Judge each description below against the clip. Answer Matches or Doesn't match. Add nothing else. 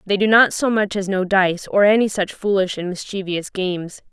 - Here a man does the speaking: Doesn't match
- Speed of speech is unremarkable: Doesn't match